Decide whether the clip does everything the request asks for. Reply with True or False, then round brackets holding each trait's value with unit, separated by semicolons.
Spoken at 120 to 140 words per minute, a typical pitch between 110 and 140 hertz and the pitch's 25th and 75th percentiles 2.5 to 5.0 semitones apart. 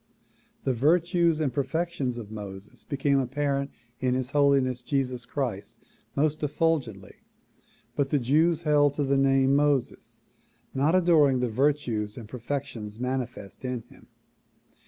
True (135 wpm; 135 Hz; 2.9 semitones)